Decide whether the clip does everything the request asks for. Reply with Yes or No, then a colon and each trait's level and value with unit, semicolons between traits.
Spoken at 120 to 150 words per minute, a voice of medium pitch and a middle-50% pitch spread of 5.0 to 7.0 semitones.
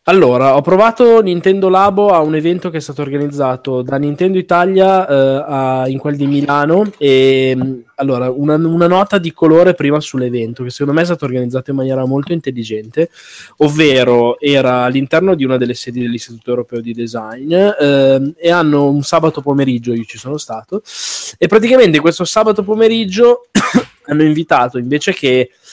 No: average, 165 wpm; medium, 145 Hz; average, 5.3 semitones